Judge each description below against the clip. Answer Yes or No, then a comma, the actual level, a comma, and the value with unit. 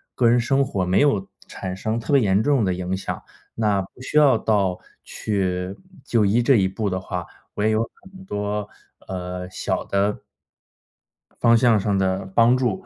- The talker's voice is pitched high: No, low, 105 Hz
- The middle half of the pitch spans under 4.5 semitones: Yes, average, 3.8 semitones